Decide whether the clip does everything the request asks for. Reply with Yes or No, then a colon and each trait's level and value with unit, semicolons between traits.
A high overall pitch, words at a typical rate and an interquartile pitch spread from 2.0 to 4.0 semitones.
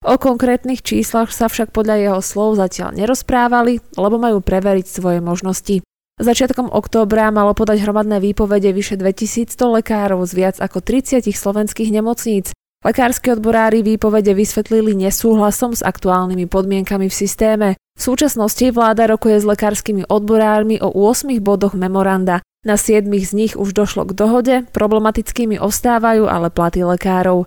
Yes: high, 210 Hz; average, 140 wpm; narrow, 2.5 semitones